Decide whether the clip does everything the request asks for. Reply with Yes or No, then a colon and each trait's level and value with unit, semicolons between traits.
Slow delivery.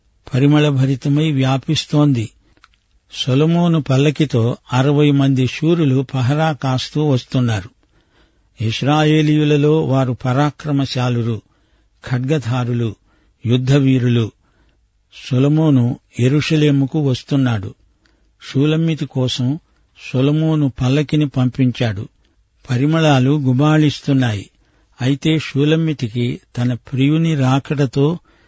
Yes: slow, 65 wpm